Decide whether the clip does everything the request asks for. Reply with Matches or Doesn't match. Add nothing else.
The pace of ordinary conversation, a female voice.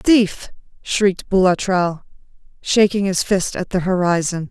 Doesn't match